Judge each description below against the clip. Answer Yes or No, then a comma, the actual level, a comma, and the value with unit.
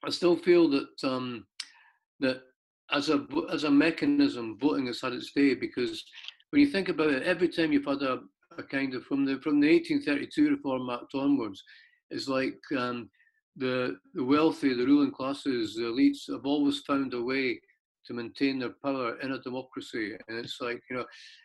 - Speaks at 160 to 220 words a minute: Yes, average, 185 wpm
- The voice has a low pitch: No, medium, 150 Hz